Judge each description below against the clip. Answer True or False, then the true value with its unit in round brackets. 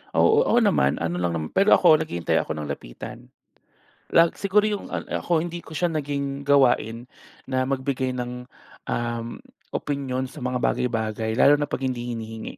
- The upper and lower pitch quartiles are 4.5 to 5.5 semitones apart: True (4.8 semitones)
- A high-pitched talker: False (130 Hz)